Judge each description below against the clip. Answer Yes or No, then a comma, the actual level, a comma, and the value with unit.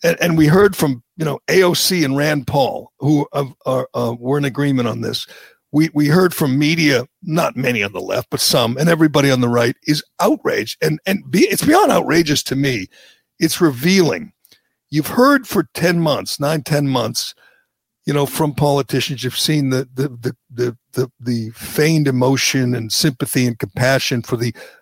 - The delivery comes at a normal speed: Yes, average, 190 wpm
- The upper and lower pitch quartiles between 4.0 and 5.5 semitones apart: No, average, 3.6 semitones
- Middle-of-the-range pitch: Yes, medium, 145 Hz